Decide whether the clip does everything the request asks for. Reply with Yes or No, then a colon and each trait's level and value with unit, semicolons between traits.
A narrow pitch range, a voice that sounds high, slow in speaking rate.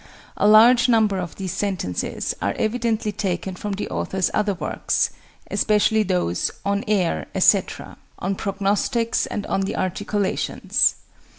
Yes: narrow, 2.3 semitones; high, 200 Hz; slow, 130 wpm